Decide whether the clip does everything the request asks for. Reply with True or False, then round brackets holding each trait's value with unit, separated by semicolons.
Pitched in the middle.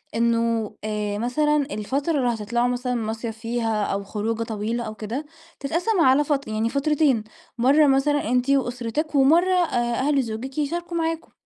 False (245 Hz)